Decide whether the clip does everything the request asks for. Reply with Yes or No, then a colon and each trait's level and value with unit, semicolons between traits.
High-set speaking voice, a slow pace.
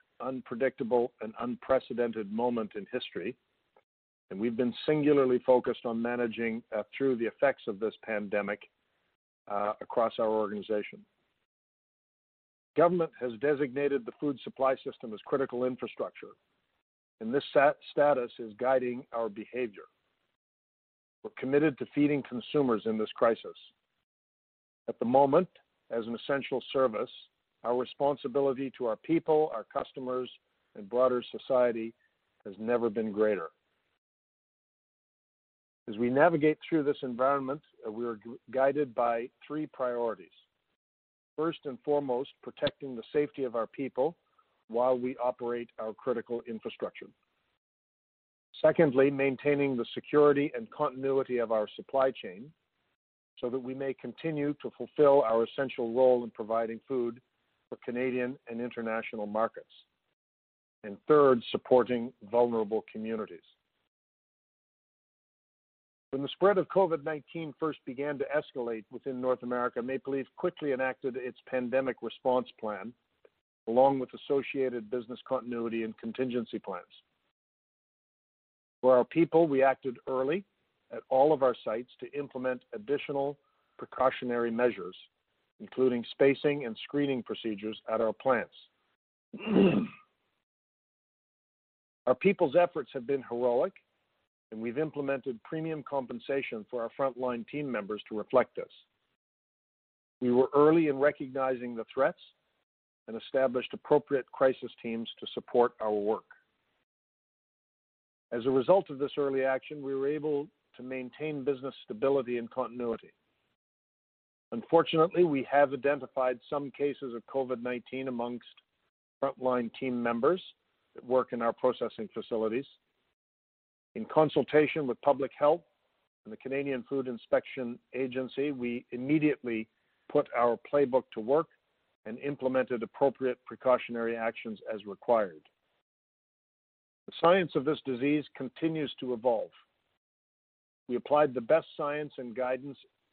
No: low, 130 Hz; slow, 125 wpm